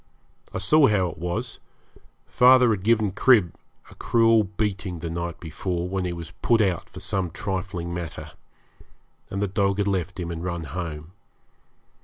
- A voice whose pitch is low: Yes, very low, 95 Hz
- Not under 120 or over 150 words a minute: No, average, 165 wpm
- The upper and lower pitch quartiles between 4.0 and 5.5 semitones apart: No, average, 3.5 semitones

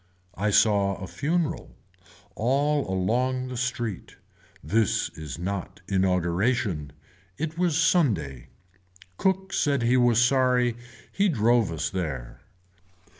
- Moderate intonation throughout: No, wide, 6.4 semitones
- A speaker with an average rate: No, slow, 110 wpm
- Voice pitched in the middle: No, low, 115 Hz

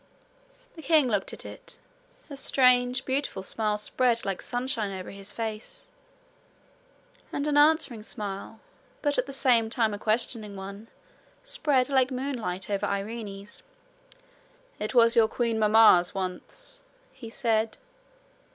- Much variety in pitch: No, average, 4.0 semitones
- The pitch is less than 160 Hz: No, high, 230 Hz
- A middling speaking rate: No, slow, 130 wpm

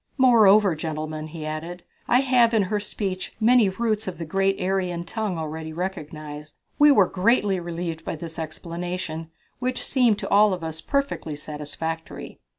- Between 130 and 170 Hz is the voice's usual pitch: No, medium, 180 Hz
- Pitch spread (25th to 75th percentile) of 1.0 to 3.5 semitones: No, average, 4.8 semitones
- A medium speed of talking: Yes, average, 155 wpm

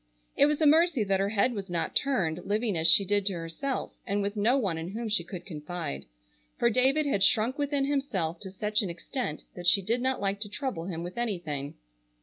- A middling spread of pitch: No, wide, 6.2 semitones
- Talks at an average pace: No, fast, 220 wpm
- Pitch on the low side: No, high, 205 Hz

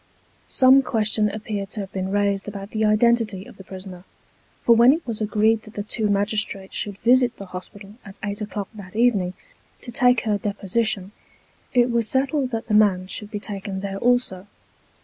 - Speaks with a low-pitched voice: No, high, 210 Hz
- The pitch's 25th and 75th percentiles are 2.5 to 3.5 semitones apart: Yes, average, 2.8 semitones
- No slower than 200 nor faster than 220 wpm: No, average, 185 wpm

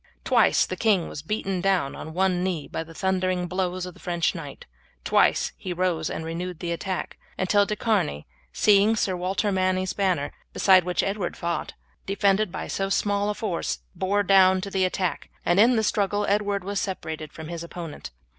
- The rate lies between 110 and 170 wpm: No, average, 190 wpm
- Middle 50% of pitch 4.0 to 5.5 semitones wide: No, narrow, 2.5 semitones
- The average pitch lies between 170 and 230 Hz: Yes, medium, 185 Hz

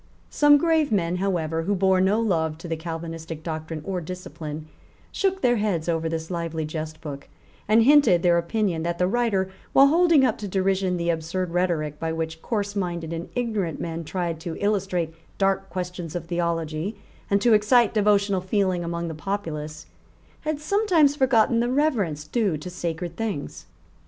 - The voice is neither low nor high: Yes, medium, 180 Hz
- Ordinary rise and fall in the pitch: Yes, average, 4.5 semitones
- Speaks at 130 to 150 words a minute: No, average, 165 wpm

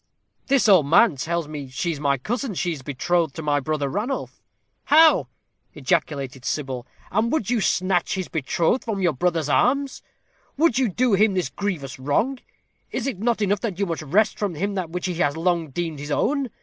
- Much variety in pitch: Yes, wide, 6.5 semitones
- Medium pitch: Yes, medium, 175 Hz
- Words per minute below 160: No, average, 195 wpm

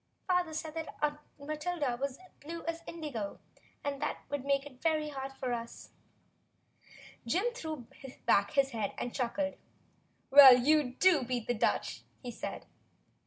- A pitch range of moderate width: Yes, average, 4.0 semitones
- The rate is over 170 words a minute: No, average, 155 wpm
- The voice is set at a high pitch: Yes, very high, 285 Hz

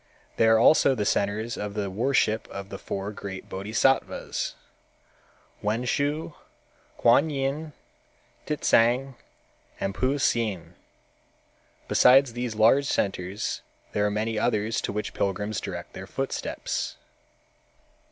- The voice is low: Yes, low, 110 Hz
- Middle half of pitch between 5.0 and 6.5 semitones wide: No, average, 4.6 semitones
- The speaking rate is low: Yes, slow, 110 wpm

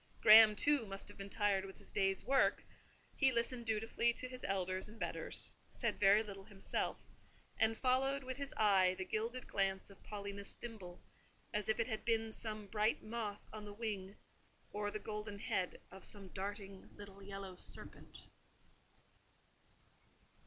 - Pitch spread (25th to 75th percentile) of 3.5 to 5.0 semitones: No, narrow, 2.4 semitones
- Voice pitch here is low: No, high, 210 Hz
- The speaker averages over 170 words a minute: No, average, 160 wpm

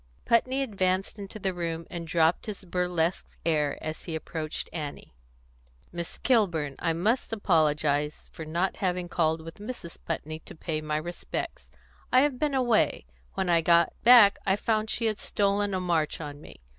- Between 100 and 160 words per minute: No, average, 170 wpm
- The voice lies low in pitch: No, medium, 175 Hz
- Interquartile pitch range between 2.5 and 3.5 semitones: No, average, 4.3 semitones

